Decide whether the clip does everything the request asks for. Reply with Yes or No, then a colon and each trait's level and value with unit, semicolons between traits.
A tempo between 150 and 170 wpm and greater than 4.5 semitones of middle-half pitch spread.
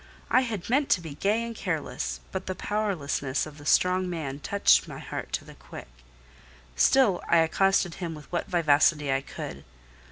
No: average, 180 wpm; average, 5.3 semitones